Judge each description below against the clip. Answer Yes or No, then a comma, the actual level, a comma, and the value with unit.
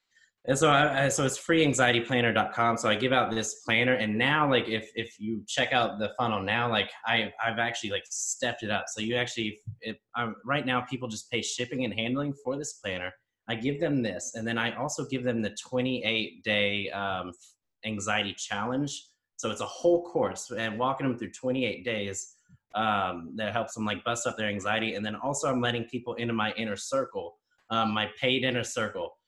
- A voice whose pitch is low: Yes, low, 115 Hz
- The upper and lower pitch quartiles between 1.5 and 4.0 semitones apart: Yes, average, 3.2 semitones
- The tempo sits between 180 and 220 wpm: Yes, fast, 205 wpm